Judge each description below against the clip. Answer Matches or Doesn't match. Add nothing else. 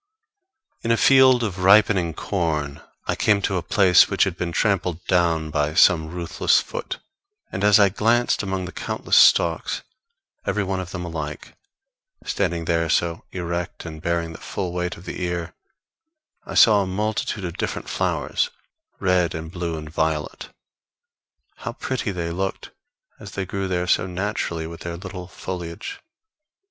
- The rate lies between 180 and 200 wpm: Doesn't match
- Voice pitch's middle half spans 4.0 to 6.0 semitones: Doesn't match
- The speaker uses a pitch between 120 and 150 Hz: Doesn't match